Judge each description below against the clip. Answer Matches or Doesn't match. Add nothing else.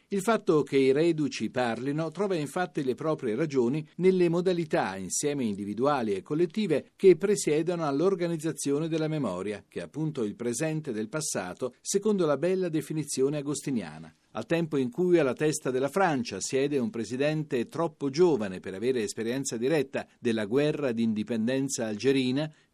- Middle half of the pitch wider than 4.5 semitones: Matches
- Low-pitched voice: Doesn't match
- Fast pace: Doesn't match